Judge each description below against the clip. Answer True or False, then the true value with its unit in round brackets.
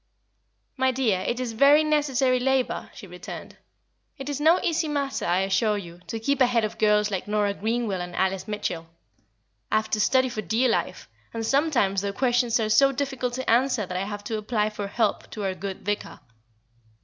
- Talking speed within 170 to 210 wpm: True (195 wpm)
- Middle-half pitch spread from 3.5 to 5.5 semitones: True (4.4 semitones)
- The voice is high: True (225 Hz)